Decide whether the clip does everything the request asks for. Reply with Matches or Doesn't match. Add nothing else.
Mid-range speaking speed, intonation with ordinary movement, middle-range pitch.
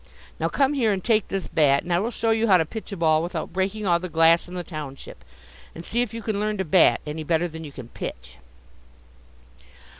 Doesn't match